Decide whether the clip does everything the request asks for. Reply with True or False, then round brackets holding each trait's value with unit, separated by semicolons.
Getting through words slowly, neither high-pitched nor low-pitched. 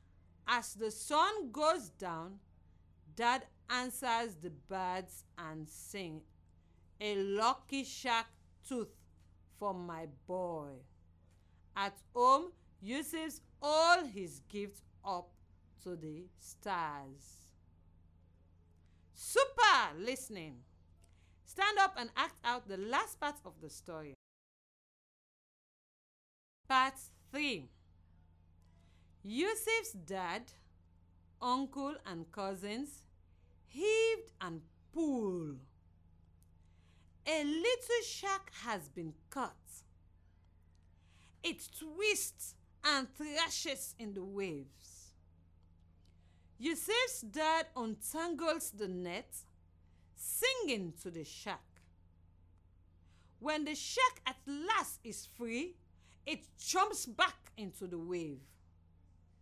True (85 wpm; 180 Hz)